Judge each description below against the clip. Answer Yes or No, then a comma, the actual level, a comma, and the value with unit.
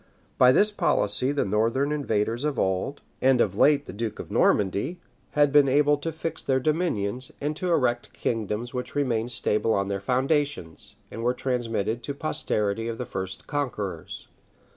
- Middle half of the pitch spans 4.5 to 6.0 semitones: Yes, average, 5.2 semitones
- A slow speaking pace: No, average, 170 wpm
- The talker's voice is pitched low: Yes, low, 125 Hz